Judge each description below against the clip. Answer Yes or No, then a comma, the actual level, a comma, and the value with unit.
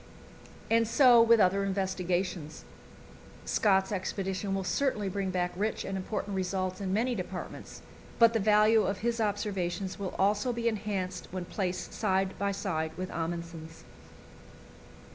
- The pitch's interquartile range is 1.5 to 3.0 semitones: Yes, narrow, 2.5 semitones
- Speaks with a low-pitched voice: No, high, 195 Hz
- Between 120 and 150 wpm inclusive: Yes, average, 140 wpm